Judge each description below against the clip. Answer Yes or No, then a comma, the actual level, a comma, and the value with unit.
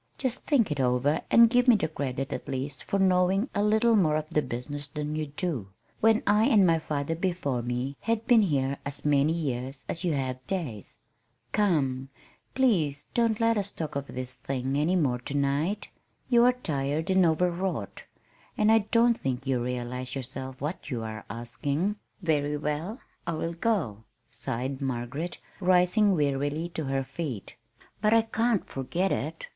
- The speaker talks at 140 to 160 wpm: No, average, 175 wpm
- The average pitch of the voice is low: No, medium, 150 Hz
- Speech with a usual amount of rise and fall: No, wide, 6.5 semitones